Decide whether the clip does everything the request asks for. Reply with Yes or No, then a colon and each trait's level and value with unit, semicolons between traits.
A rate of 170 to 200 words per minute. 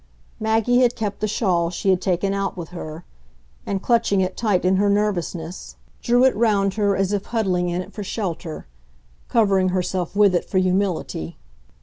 Yes: average, 180 wpm